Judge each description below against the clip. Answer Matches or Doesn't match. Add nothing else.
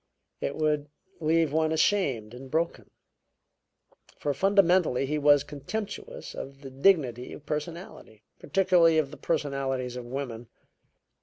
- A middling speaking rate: Doesn't match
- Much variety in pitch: Doesn't match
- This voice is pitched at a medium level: Matches